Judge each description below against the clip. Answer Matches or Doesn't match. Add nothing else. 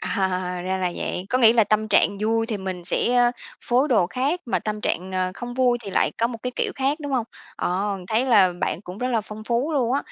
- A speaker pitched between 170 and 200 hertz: Doesn't match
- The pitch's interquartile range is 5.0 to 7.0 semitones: Doesn't match